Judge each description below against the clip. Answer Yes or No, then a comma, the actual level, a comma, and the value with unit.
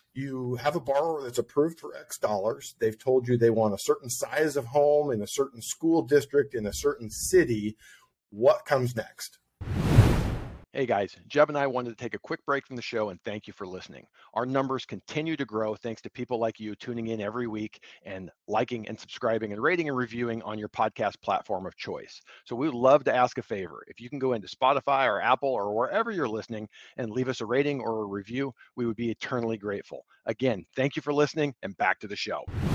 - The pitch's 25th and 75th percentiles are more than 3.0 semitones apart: Yes, average, 4.3 semitones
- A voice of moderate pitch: No, low, 125 Hz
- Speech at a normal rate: No, fast, 220 wpm